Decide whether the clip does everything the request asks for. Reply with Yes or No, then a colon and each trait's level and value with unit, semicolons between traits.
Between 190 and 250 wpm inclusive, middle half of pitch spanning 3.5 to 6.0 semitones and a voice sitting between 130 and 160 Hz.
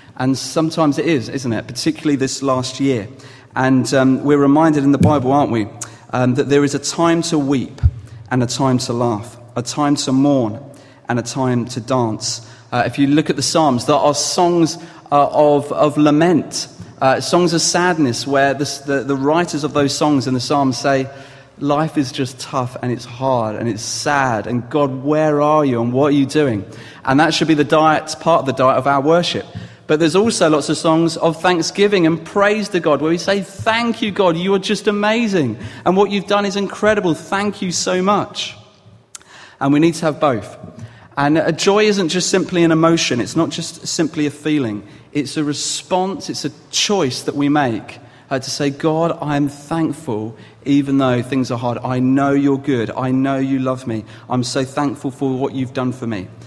Yes: fast, 205 wpm; average, 3.9 semitones; medium, 140 Hz